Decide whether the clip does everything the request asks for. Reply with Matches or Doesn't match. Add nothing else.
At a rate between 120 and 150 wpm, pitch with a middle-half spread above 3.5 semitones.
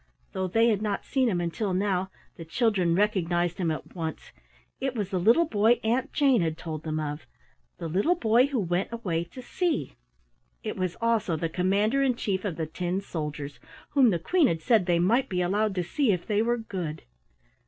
Doesn't match